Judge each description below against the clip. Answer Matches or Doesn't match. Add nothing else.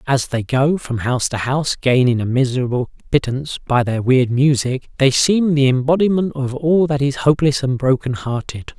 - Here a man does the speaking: Matches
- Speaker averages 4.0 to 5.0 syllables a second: Doesn't match